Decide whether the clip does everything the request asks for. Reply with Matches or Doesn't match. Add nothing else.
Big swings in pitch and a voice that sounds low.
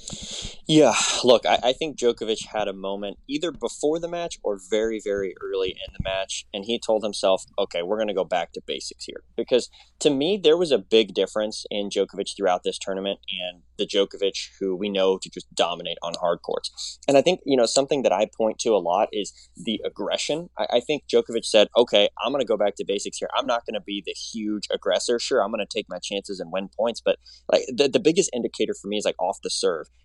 Matches